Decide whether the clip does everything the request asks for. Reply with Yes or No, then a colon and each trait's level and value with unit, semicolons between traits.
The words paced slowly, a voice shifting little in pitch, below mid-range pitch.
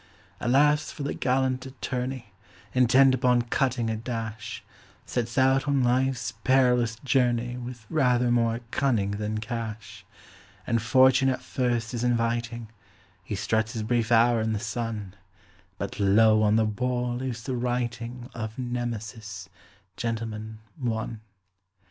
Yes: slow, 130 wpm; narrow, 2.2 semitones; low, 120 Hz